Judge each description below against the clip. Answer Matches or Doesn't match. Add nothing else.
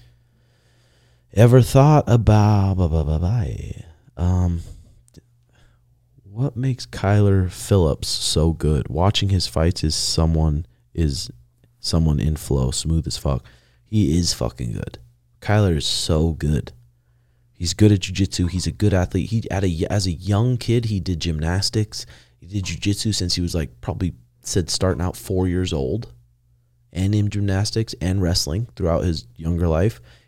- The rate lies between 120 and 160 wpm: Matches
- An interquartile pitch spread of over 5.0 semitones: Matches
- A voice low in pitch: Matches